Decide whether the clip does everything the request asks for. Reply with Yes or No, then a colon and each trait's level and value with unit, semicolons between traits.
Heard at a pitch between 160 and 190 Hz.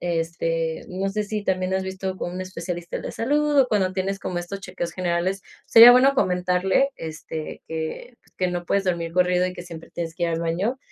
Yes: medium, 185 Hz